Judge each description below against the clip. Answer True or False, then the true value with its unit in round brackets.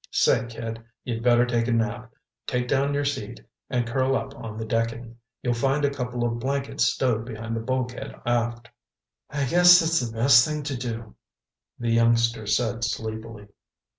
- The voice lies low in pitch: True (120 Hz)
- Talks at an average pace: True (170 wpm)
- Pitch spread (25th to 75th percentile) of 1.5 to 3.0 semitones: True (2.4 semitones)